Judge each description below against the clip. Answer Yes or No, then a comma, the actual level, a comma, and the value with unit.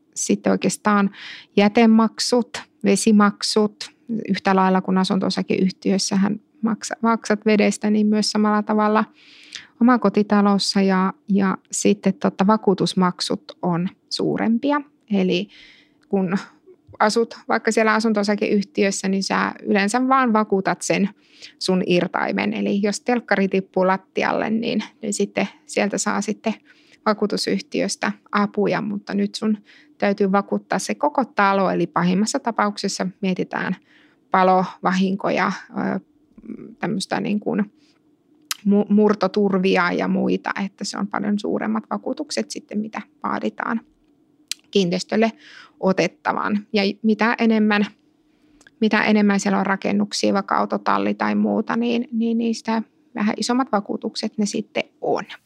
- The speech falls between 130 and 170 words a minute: No, average, 110 wpm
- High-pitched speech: Yes, high, 210 Hz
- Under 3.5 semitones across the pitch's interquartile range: Yes, average, 2.8 semitones